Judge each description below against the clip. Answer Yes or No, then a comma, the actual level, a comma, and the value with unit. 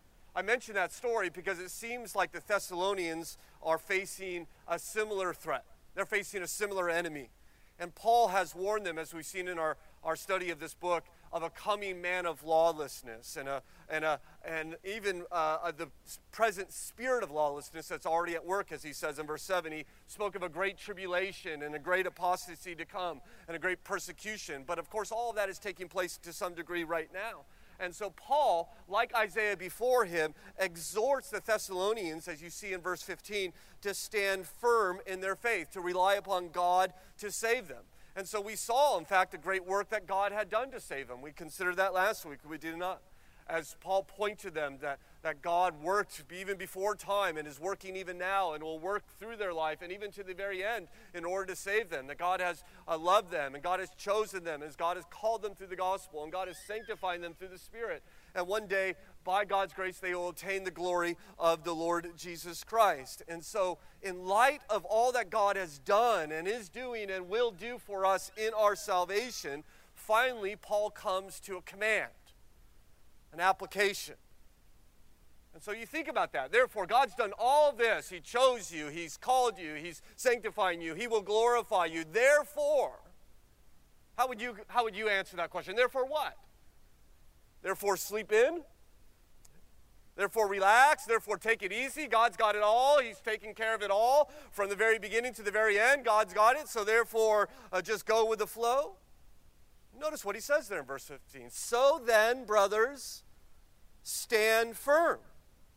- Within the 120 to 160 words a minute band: No, average, 190 wpm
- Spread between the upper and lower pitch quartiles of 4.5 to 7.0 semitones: No, average, 4.0 semitones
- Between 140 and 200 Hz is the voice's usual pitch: Yes, high, 190 Hz